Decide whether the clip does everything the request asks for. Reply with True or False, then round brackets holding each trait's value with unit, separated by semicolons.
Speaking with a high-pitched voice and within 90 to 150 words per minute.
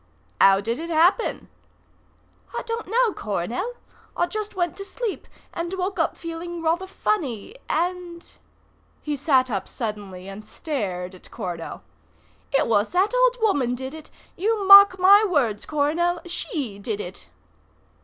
True (330 Hz; 145 wpm)